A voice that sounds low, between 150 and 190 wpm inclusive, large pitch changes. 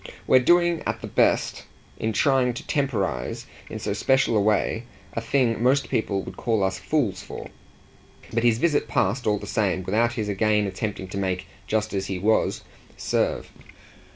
No: low, 110 Hz; average, 175 wpm; average, 4.1 semitones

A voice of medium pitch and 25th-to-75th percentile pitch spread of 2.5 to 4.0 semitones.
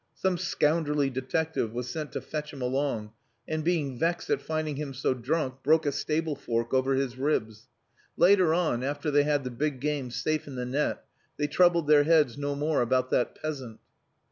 Yes: medium, 145 Hz; average, 3.2 semitones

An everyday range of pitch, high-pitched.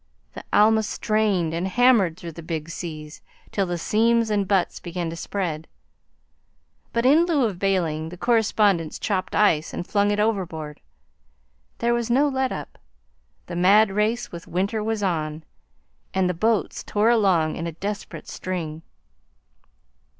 Yes: average, 4.6 semitones; high, 195 Hz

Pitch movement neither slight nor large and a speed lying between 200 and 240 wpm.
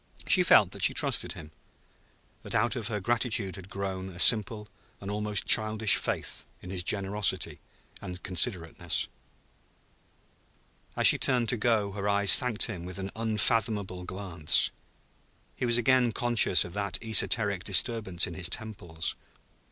No: average, 3.2 semitones; average, 145 wpm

